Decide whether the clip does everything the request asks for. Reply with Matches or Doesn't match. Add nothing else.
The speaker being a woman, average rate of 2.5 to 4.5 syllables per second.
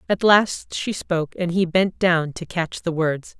Matches